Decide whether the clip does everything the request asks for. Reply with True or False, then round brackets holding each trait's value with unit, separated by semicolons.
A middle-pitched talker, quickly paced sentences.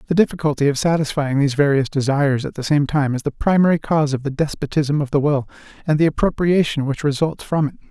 True (145 Hz; 210 wpm)